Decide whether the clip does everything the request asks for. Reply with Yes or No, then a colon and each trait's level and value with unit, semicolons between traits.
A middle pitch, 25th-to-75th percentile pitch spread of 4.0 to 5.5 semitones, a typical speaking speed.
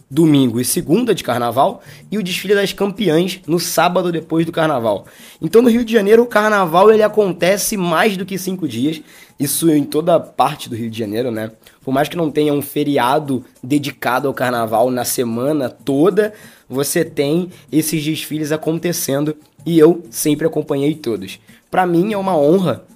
Yes: medium, 155 Hz; average, 4.4 semitones; average, 175 wpm